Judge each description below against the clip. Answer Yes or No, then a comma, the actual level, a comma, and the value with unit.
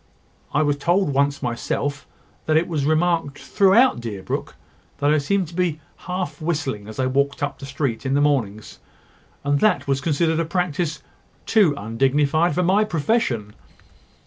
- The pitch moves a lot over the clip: No, average, 3.9 semitones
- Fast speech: No, average, 165 wpm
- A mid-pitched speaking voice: Yes, medium, 145 Hz